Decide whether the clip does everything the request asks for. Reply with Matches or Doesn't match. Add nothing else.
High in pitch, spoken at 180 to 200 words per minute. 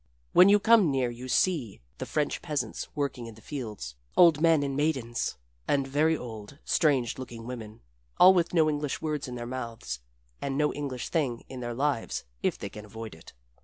Doesn't match